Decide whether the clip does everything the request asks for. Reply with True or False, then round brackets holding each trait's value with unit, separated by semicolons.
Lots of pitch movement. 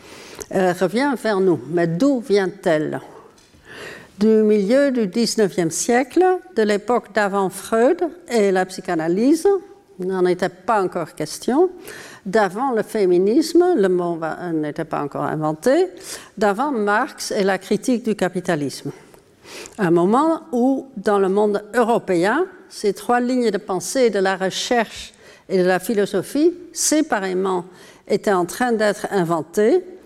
True (6.3 semitones)